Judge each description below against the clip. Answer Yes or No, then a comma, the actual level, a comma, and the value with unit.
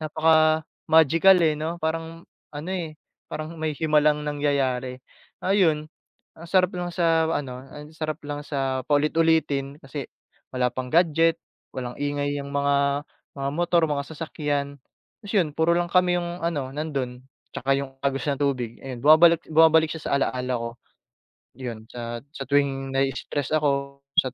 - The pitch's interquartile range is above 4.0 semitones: No, average, 2.9 semitones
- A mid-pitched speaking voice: Yes, medium, 150 Hz